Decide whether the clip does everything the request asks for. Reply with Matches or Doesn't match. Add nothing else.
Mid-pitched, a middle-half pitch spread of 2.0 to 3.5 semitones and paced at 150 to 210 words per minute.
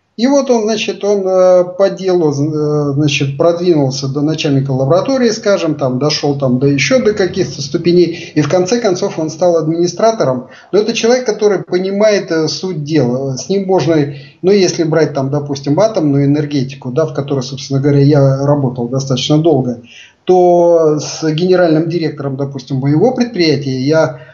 Doesn't match